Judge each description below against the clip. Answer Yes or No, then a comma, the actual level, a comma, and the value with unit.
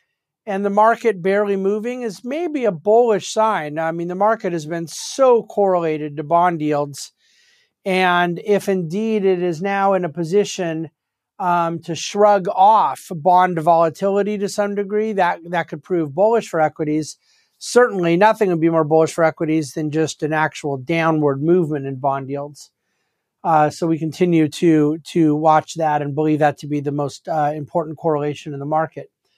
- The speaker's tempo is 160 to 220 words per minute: Yes, average, 170 wpm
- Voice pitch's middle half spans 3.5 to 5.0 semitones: Yes, average, 4.5 semitones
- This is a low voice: No, medium, 170 Hz